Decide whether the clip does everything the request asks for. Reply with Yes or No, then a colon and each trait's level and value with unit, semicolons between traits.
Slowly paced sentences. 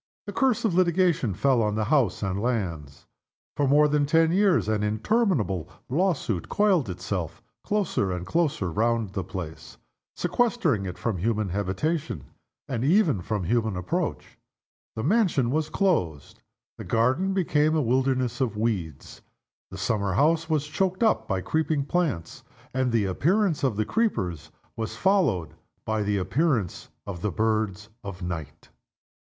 No: average, 145 wpm